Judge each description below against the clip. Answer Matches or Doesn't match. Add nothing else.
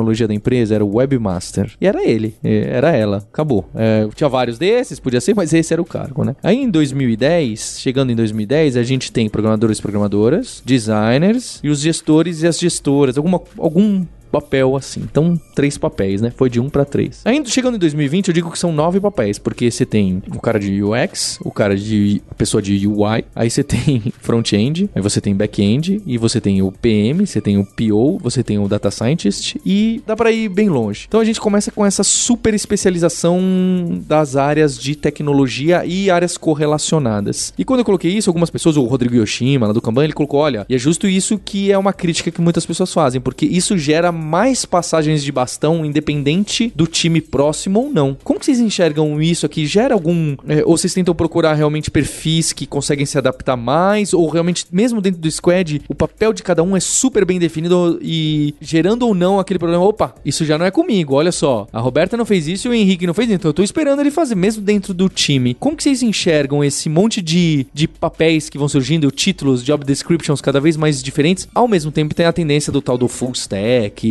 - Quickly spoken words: Matches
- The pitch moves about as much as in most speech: Doesn't match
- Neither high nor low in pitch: Matches